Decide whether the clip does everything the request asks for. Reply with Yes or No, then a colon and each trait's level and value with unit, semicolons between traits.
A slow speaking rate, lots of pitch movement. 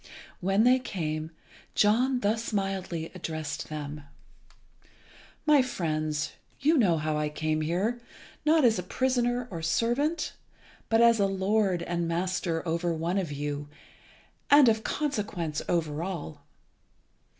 Yes: slow, 130 wpm; wide, 6.6 semitones